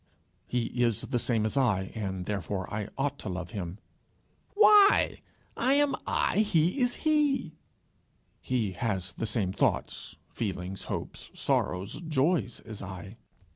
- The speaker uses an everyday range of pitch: No, wide, 9.0 semitones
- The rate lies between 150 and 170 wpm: No, slow, 135 wpm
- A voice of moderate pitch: No, low, 115 Hz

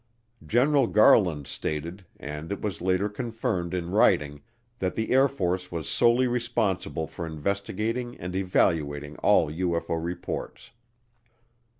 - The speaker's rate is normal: No, slow, 120 wpm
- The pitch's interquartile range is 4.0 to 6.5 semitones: Yes, average, 5.3 semitones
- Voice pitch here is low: Yes, very low, 95 Hz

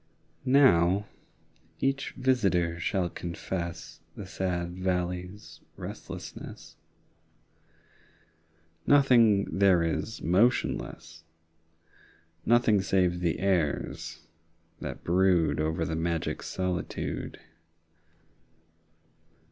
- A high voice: No, very low, 90 Hz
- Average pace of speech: No, slow, 75 wpm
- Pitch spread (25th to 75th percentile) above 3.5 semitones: No, average, 2.7 semitones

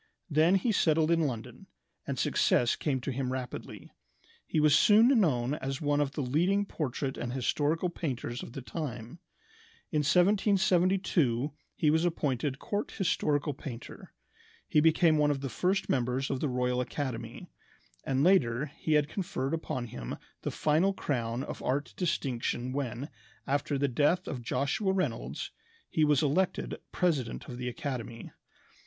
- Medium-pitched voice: Yes, medium, 145 Hz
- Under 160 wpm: Yes, average, 150 wpm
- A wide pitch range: No, average, 4.5 semitones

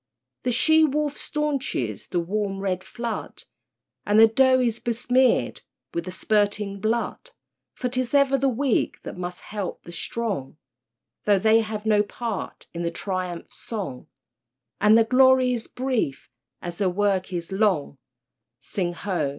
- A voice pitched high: Yes, high, 215 Hz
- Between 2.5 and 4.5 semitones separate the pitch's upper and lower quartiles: No, average, 5.2 semitones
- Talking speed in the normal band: Yes, average, 150 wpm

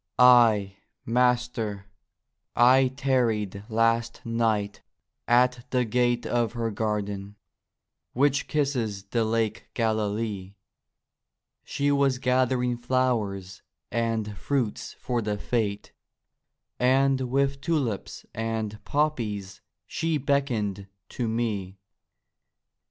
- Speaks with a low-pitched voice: Yes, low, 115 Hz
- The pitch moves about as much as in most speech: Yes, average, 3.3 semitones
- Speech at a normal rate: No, slow, 90 wpm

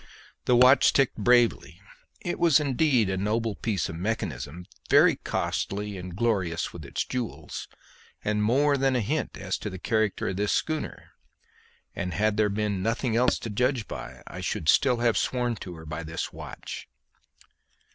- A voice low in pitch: Yes, low, 110 Hz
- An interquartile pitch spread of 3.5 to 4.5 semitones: No, average, 5.0 semitones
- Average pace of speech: Yes, average, 165 wpm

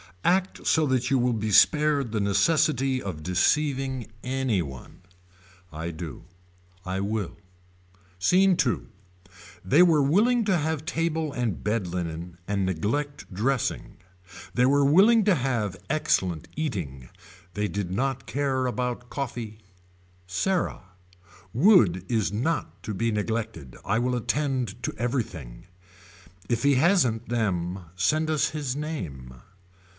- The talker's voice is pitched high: No, low, 120 Hz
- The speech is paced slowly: Yes, slow, 125 wpm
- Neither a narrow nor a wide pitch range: No, wide, 7.2 semitones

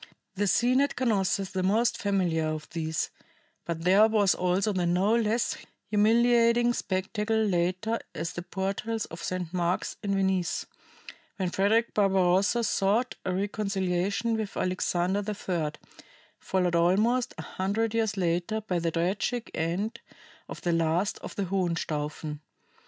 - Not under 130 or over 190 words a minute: Yes, average, 140 wpm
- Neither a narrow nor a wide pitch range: Yes, average, 3.6 semitones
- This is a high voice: Yes, high, 195 Hz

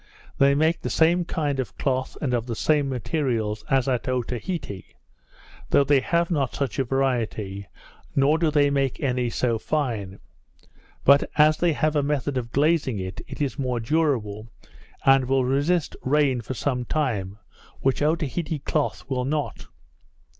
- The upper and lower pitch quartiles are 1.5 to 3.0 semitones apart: No, average, 3.4 semitones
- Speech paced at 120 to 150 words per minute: No, average, 160 wpm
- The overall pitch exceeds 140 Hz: No, low, 135 Hz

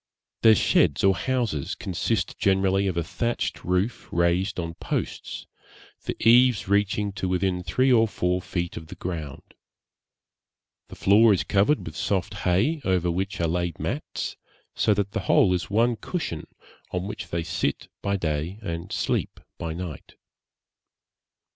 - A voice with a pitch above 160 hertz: No, very low, 95 Hz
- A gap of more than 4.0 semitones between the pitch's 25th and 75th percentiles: No, average, 3.2 semitones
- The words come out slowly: No, average, 150 wpm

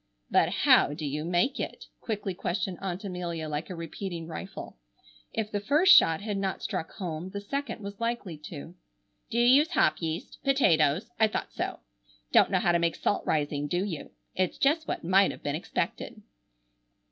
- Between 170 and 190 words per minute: Yes, average, 180 wpm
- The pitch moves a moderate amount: Yes, average, 4.9 semitones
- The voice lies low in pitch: No, medium, 185 Hz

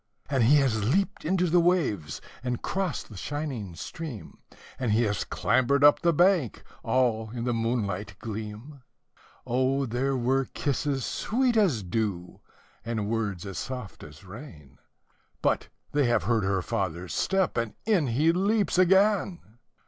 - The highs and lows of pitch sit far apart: Yes, wide, 6.4 semitones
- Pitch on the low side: Yes, low, 125 Hz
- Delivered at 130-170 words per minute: Yes, average, 150 wpm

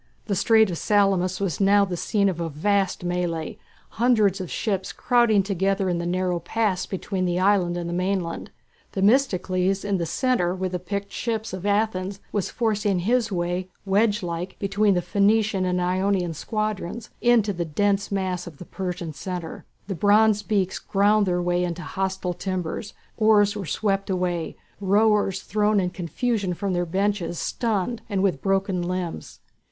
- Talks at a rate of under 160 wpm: No, average, 165 wpm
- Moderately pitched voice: No, high, 195 Hz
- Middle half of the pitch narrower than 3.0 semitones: Yes, narrow, 2.5 semitones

